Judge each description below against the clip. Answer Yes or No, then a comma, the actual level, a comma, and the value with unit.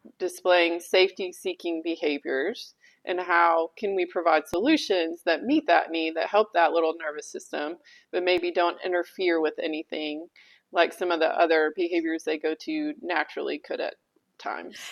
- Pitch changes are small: Yes, narrow, 2.2 semitones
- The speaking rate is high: No, average, 155 wpm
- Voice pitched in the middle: Yes, medium, 170 Hz